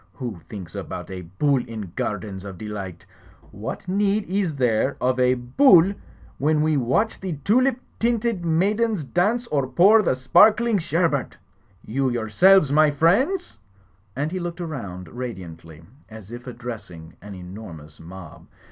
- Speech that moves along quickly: No, average, 145 wpm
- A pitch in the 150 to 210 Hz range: No, low, 130 Hz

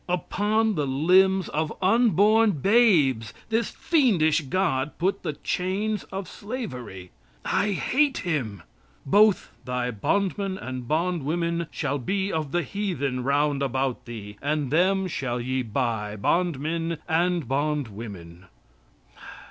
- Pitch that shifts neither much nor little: No, wide, 6.7 semitones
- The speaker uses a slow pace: Yes, slow, 115 wpm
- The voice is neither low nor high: Yes, medium, 160 Hz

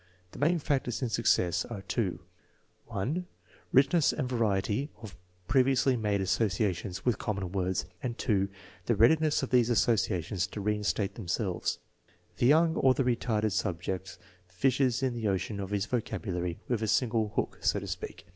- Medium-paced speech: Yes, average, 165 wpm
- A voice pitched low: Yes, low, 110 Hz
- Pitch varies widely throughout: No, average, 4.7 semitones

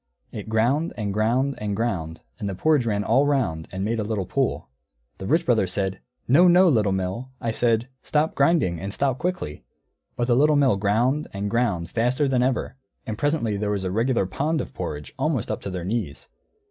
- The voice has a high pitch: No, low, 115 Hz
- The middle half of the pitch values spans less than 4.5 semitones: No, wide, 5.5 semitones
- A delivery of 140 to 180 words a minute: No, average, 200 wpm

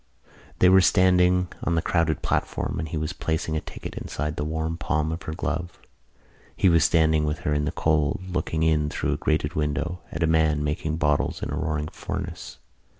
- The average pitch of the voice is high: No, very low, 80 Hz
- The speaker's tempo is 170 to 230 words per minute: Yes, average, 200 wpm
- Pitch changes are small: Yes, narrow, 1.7 semitones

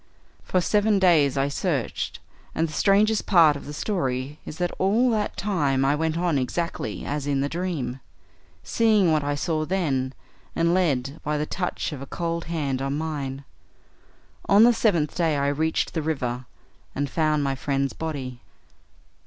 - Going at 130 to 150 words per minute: No, average, 170 wpm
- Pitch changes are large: No, average, 4.3 semitones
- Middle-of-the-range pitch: Yes, medium, 155 Hz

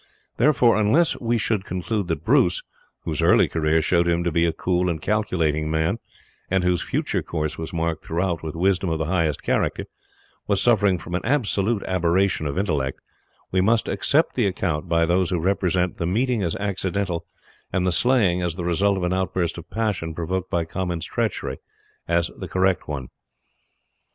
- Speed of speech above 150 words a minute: Yes, average, 180 wpm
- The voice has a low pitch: Yes, very low, 90 Hz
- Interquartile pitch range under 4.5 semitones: Yes, average, 3.0 semitones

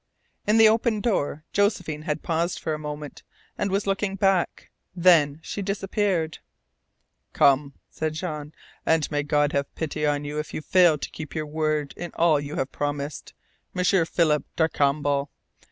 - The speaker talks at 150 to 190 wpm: Yes, average, 160 wpm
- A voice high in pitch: No, medium, 155 Hz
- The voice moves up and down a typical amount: Yes, average, 3.8 semitones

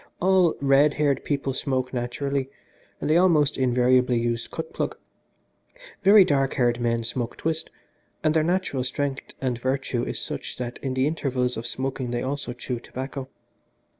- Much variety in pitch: No, average, 2.8 semitones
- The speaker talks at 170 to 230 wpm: No, average, 160 wpm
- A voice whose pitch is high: No, low, 135 Hz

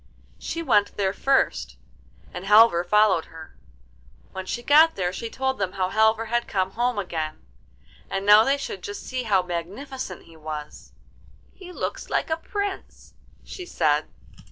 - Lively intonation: Yes, wide, 5.9 semitones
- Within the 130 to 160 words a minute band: Yes, average, 155 wpm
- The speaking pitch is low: No, high, 210 Hz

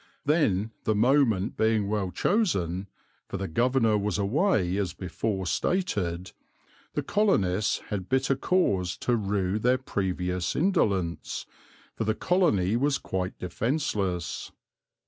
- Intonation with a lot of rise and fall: Yes, wide, 6.1 semitones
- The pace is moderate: No, slow, 120 wpm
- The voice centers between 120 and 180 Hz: No, low, 105 Hz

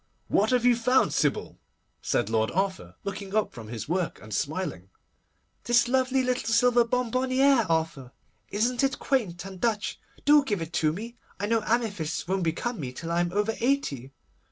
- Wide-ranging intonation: Yes, wide, 7.0 semitones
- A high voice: Yes, high, 205 Hz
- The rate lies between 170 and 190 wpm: Yes, average, 175 wpm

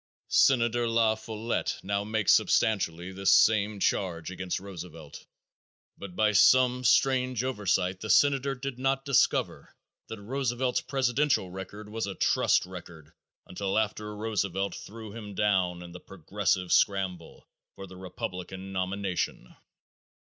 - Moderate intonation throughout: Yes, average, 3.8 semitones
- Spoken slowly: Yes, slow, 130 wpm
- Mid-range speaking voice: No, low, 100 Hz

